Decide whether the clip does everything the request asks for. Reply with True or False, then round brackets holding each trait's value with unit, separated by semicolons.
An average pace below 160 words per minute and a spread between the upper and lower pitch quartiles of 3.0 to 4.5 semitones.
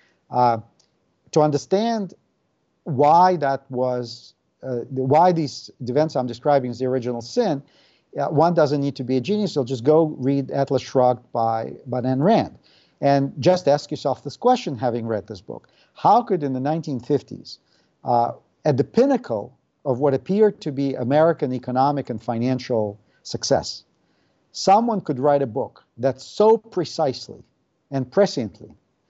True (145 wpm; 3.6 semitones)